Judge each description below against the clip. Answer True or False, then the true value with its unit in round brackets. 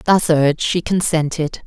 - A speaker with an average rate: True (145 wpm)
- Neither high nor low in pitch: True (160 Hz)